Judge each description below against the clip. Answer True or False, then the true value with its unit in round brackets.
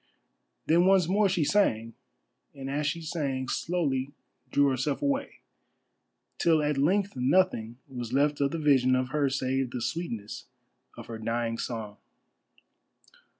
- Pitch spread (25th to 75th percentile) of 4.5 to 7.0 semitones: True (4.8 semitones)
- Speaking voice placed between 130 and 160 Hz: True (140 Hz)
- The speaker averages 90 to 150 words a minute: True (140 wpm)